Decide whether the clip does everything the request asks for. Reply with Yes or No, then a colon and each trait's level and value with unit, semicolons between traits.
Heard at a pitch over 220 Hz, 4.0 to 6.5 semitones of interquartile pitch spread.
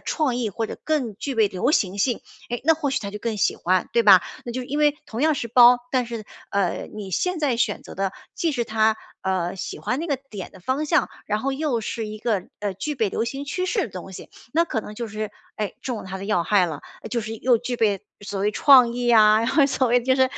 Yes: high, 230 Hz; average, 4.3 semitones